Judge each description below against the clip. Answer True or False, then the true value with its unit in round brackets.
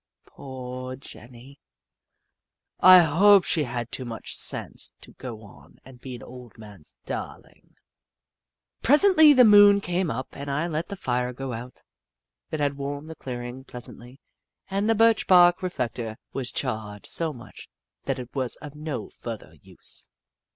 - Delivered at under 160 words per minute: True (150 wpm)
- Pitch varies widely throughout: True (6.0 semitones)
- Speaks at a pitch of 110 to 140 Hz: True (135 Hz)